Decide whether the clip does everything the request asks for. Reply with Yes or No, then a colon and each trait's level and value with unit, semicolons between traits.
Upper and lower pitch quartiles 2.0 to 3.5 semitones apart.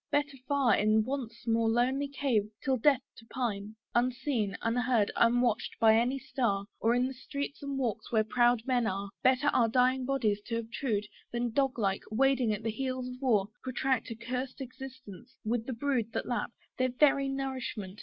Yes: average, 3.0 semitones